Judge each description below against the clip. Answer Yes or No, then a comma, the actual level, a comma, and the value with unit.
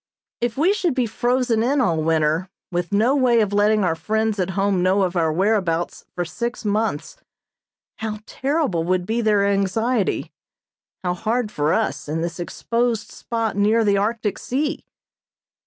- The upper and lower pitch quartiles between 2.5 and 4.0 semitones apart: No, average, 4.5 semitones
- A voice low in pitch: No, high, 210 Hz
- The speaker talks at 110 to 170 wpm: Yes, average, 160 wpm